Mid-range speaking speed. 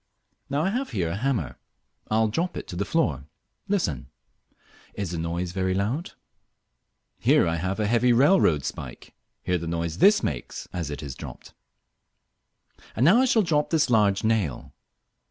Yes: average, 170 wpm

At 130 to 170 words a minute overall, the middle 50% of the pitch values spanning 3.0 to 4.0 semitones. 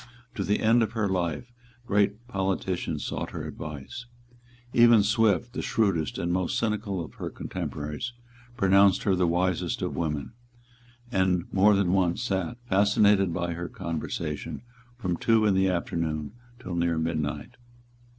Yes: average, 145 wpm; average, 3.7 semitones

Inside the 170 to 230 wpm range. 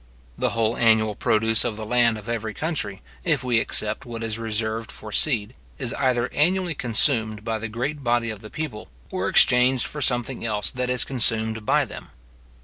Yes: average, 185 wpm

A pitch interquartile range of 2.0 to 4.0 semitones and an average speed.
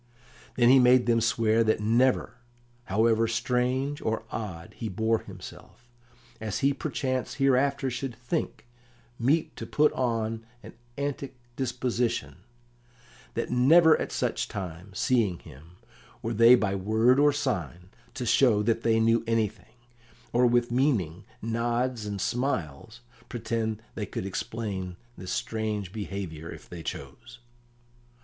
No: average, 3.2 semitones; slow, 130 wpm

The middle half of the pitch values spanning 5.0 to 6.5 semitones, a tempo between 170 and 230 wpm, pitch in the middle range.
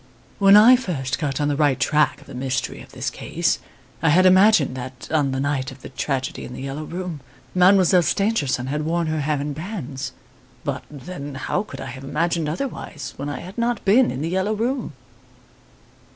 Yes: wide, 5.4 semitones; average, 195 wpm; medium, 150 Hz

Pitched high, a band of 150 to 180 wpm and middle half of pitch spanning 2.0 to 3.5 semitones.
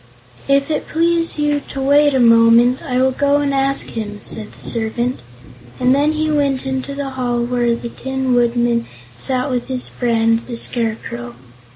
Yes: very high, 255 Hz; average, 175 wpm; average, 2.9 semitones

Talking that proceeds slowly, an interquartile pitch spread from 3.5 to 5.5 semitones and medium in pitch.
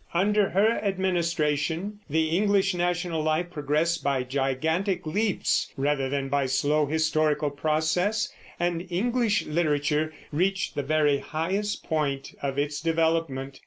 Yes: slow, 125 wpm; average, 3.9 semitones; medium, 160 Hz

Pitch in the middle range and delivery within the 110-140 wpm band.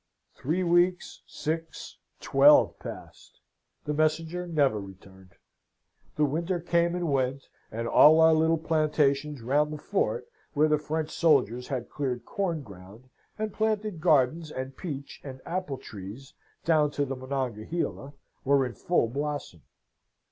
Yes: medium, 150 Hz; slow, 135 wpm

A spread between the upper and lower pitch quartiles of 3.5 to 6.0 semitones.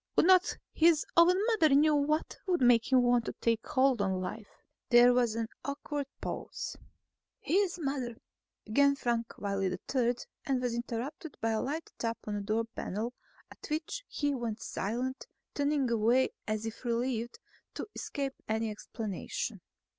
Yes: average, 4.1 semitones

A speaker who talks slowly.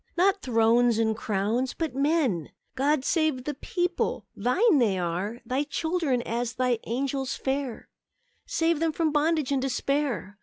No: average, 145 wpm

